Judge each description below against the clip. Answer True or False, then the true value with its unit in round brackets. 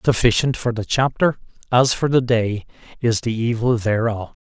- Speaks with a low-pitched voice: True (115 Hz)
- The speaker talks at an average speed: True (160 wpm)